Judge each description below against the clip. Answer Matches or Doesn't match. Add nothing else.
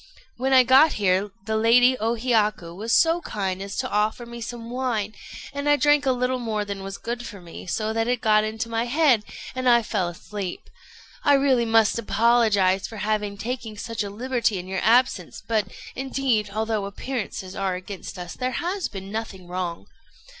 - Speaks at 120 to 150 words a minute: Doesn't match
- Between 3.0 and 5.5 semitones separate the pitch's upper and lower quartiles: Matches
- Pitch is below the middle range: Doesn't match